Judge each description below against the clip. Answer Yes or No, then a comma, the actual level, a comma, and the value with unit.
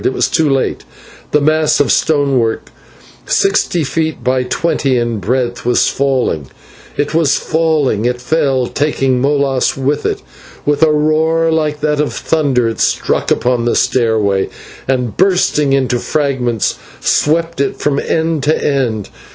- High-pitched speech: No, medium, 140 Hz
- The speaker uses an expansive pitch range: No, average, 3.8 semitones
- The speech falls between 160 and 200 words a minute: No, average, 150 wpm